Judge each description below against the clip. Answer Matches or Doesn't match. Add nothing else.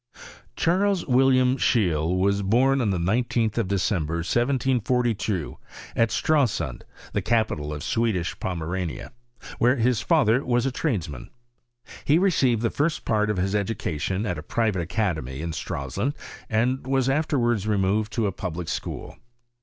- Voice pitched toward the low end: Matches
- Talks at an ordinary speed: Matches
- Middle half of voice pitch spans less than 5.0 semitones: Doesn't match